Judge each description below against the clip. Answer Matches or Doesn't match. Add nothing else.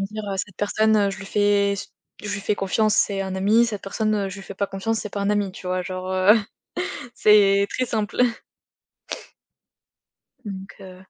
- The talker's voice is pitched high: Matches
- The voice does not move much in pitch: Matches